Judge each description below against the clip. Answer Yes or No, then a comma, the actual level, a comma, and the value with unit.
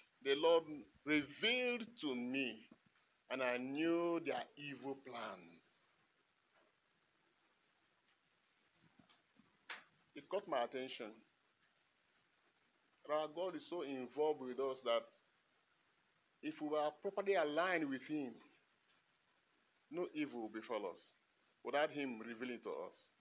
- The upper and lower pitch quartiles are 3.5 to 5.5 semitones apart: Yes, average, 4.9 semitones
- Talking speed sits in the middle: No, slow, 105 wpm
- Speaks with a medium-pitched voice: Yes, medium, 150 Hz